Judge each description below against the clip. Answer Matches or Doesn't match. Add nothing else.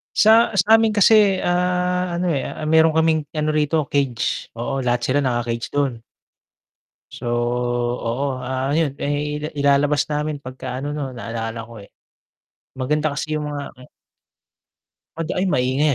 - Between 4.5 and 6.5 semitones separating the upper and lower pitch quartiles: Doesn't match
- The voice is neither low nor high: Matches